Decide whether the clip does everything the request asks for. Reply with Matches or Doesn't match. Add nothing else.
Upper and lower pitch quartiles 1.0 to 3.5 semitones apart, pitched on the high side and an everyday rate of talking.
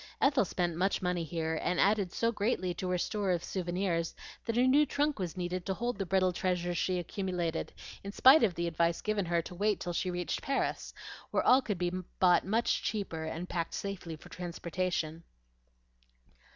Doesn't match